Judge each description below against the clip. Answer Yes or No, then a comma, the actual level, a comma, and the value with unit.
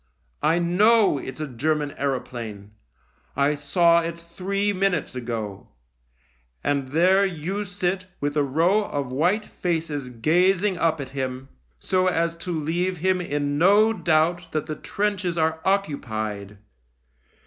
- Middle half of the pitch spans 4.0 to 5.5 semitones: Yes, average, 4.9 semitones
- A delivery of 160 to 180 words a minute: No, average, 140 wpm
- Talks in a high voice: No, medium, 160 Hz